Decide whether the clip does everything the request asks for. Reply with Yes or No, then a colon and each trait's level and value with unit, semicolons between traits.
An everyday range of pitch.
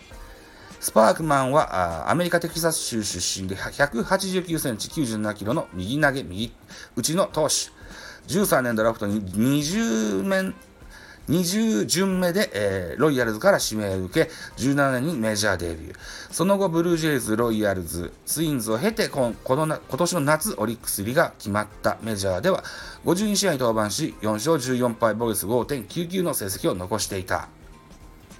No: wide, 8.4 semitones